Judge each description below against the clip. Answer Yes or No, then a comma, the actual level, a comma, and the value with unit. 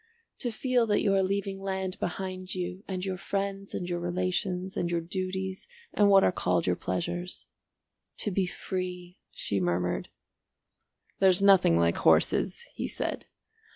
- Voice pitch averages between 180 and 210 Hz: Yes, medium, 185 Hz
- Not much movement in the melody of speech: Yes, narrow, 1.8 semitones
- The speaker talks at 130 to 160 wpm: Yes, average, 155 wpm